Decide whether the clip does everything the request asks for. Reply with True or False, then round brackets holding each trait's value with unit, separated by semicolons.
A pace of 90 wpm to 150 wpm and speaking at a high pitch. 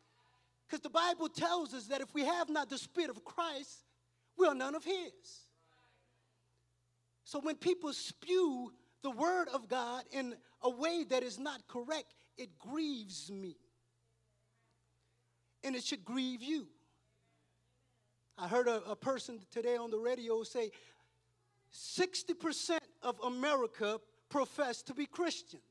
True (140 wpm; 250 Hz)